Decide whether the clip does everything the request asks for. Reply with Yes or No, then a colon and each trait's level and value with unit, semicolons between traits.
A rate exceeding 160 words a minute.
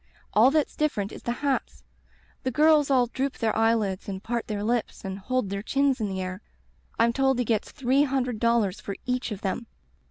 Yes: average, 200 wpm